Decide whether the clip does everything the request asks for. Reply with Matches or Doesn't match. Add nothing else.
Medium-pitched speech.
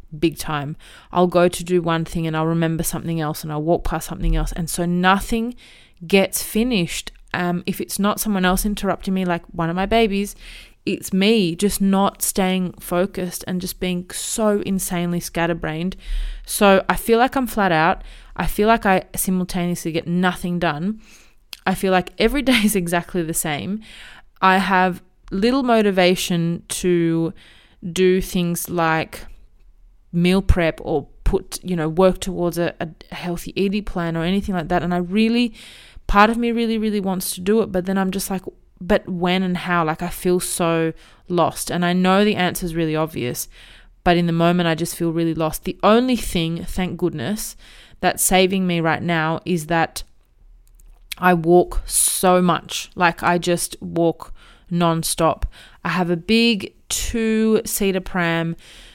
Matches